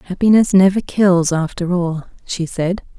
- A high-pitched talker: No, medium, 180 Hz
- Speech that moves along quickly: No, average, 140 wpm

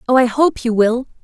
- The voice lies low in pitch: No, high, 245 Hz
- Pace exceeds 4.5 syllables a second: No, 4.4 syllables/s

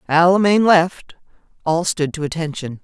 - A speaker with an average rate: Yes, average, 170 wpm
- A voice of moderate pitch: Yes, medium, 165 Hz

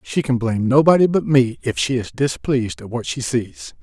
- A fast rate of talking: Yes, fast, 220 wpm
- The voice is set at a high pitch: No, low, 120 Hz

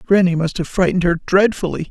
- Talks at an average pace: Yes, average, 190 wpm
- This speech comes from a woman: No, male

